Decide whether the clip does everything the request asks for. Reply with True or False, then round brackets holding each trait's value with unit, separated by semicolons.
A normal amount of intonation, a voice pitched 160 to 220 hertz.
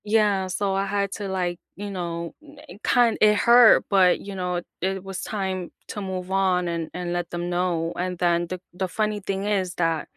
False (2.3 semitones; 190 Hz)